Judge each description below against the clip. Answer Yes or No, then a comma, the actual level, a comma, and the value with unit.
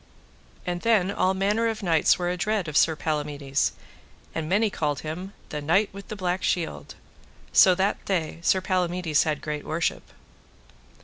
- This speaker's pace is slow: No, average, 160 wpm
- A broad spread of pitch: No, average, 3.7 semitones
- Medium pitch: Yes, medium, 180 Hz